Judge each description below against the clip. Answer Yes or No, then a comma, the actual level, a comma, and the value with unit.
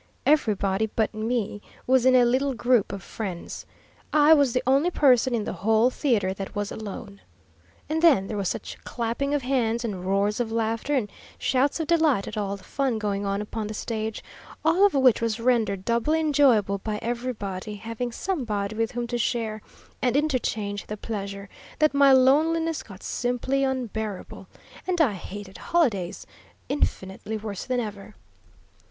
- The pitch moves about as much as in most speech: Yes, average, 4.4 semitones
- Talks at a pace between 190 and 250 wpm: No, average, 165 wpm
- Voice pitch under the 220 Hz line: No, high, 230 Hz